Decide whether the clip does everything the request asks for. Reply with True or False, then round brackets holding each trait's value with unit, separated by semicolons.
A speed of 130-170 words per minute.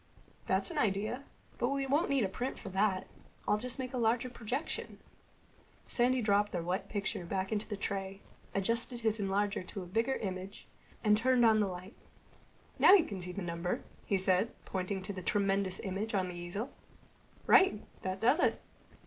False (185 wpm)